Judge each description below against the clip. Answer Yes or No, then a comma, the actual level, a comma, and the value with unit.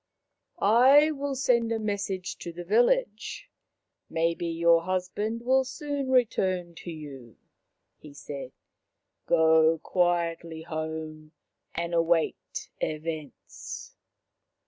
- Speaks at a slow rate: Yes, slow, 110 wpm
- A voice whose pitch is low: No, medium, 175 Hz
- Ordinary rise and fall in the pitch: No, wide, 6.2 semitones